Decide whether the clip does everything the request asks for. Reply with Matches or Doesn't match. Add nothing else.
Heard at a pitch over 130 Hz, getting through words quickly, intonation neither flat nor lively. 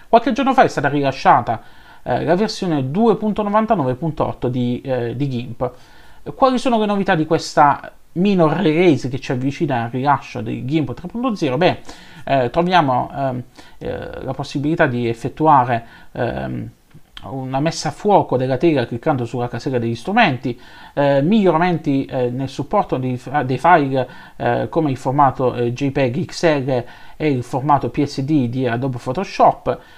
Doesn't match